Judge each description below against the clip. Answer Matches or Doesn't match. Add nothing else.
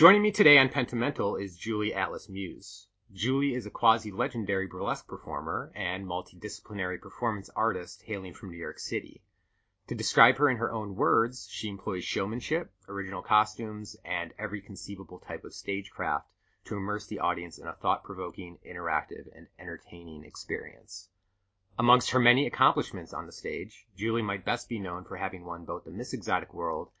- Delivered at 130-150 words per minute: Doesn't match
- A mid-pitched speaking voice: Doesn't match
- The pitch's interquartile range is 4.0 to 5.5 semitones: Doesn't match